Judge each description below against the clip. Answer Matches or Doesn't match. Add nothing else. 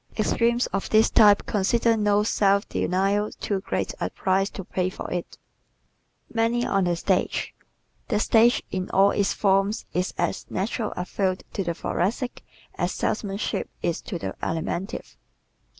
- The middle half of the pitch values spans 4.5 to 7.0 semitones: Doesn't match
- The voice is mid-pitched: Doesn't match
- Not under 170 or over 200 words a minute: Doesn't match